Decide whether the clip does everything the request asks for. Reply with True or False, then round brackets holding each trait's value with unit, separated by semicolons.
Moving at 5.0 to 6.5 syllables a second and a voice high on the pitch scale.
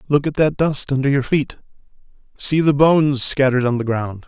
False (5.5 syllables/s; 140 Hz)